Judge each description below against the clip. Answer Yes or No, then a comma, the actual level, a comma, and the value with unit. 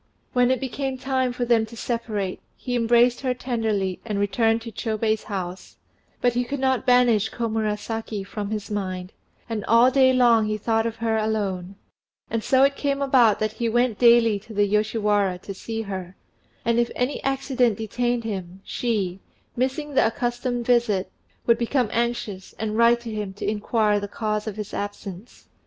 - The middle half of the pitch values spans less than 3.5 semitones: Yes, average, 2.7 semitones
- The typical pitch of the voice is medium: No, high, 225 Hz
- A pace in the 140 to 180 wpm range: Yes, average, 175 wpm